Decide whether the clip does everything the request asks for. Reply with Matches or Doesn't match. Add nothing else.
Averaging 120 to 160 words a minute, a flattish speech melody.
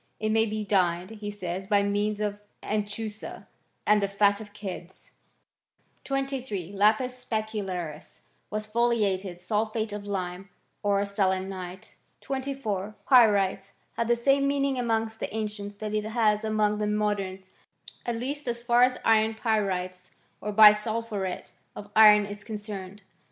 Matches